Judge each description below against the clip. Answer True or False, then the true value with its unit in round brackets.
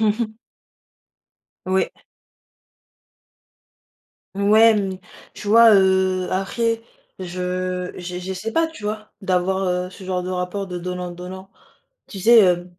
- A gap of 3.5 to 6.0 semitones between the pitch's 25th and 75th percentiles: False (2.7 semitones)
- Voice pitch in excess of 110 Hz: True (190 Hz)